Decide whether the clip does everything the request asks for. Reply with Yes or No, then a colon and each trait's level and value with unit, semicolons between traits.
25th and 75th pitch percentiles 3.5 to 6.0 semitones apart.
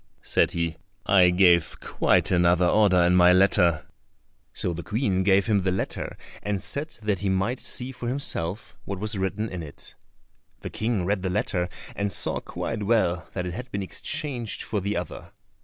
No: average, 3.1 semitones